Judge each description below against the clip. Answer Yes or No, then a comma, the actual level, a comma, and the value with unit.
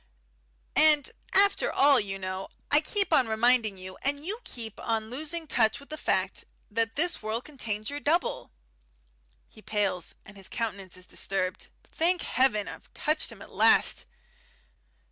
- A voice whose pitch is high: Yes, high, 230 Hz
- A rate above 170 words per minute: No, average, 155 wpm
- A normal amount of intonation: No, wide, 6.7 semitones